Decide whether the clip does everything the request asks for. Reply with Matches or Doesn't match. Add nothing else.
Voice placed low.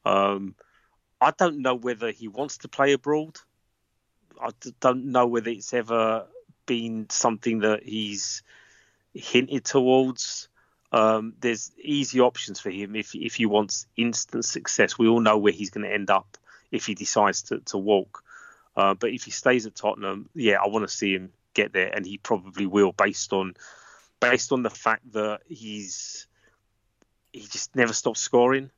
Matches